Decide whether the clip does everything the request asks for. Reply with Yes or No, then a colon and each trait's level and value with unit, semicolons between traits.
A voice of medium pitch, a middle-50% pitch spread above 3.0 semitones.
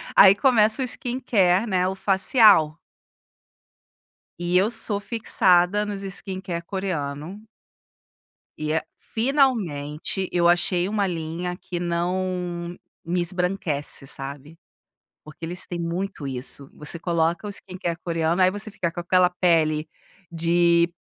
No: medium, 180 Hz; average, 2.7 semitones